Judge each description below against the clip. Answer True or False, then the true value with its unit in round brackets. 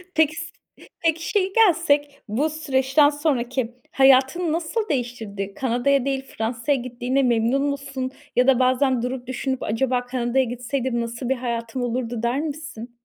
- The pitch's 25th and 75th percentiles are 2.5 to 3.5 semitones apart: True (3.1 semitones)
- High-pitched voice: True (260 Hz)